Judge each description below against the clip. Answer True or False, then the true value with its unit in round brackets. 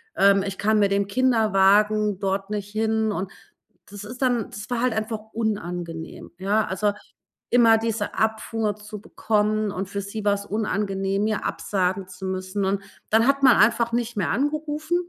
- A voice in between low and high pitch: False (210 Hz)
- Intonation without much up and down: True (2.1 semitones)